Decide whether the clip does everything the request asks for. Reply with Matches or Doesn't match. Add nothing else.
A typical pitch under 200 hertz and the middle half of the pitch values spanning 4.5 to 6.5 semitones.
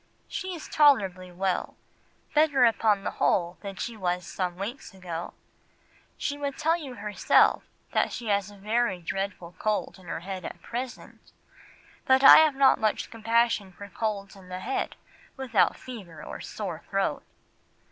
Doesn't match